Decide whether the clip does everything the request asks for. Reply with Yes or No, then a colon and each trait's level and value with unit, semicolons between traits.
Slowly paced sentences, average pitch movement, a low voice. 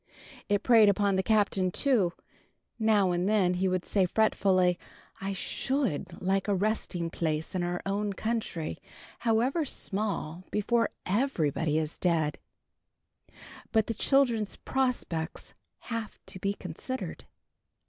No: slow, 125 wpm; average, 3.8 semitones; high, 200 Hz